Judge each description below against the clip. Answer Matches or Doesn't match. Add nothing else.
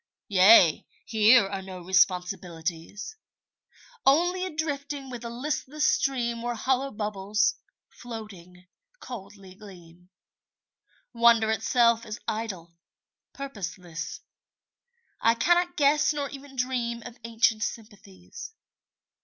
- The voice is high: Matches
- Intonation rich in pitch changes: Matches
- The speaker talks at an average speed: Doesn't match